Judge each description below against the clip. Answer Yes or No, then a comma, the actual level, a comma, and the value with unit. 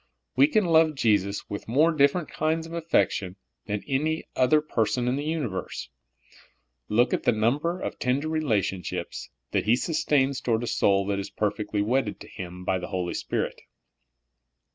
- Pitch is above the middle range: No, low, 125 Hz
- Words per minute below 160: No, average, 165 wpm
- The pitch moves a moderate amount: No, wide, 7.0 semitones